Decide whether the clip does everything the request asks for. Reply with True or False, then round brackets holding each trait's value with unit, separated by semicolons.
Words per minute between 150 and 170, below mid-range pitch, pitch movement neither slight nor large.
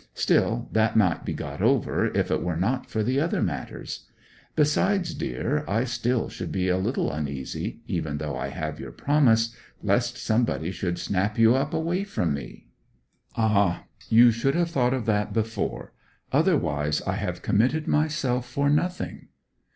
False (160 wpm; 115 Hz; 6.1 semitones)